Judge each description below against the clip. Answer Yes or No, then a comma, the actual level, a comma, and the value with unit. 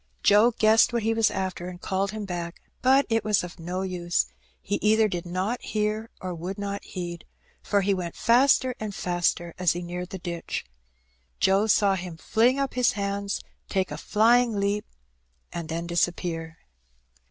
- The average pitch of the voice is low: No, high, 195 Hz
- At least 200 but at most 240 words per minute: No, average, 175 wpm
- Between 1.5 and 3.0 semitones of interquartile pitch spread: No, average, 3.6 semitones